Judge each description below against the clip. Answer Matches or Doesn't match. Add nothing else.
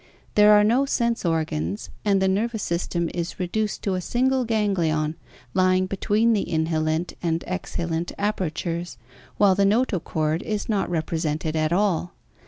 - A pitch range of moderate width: Matches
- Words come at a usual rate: Matches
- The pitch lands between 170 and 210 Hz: Matches